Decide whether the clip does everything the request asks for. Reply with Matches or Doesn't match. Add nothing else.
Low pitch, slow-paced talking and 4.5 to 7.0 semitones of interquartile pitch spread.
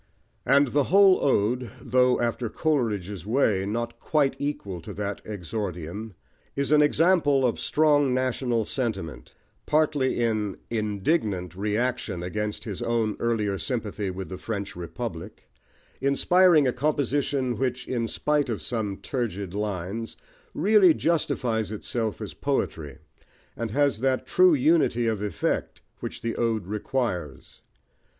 Matches